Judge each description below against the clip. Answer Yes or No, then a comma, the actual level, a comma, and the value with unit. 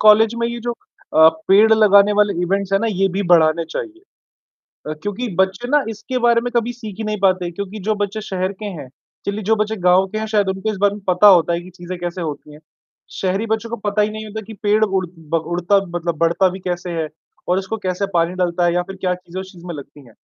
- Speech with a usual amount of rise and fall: Yes, average, 3.4 semitones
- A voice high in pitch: Yes, high, 195 Hz